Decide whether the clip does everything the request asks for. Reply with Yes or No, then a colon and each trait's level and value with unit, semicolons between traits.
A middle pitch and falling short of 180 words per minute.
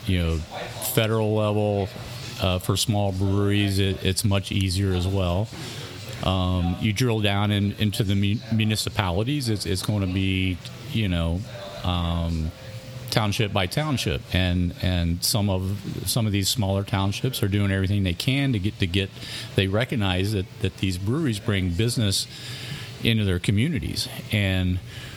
No: low, 100 Hz; average, 150 wpm